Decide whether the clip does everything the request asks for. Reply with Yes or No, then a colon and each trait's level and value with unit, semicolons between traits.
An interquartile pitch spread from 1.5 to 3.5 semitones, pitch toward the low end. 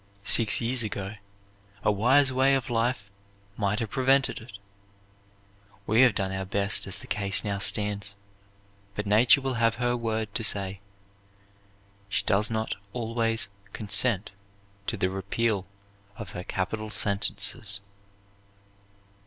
Yes: average, 2.9 semitones; low, 110 Hz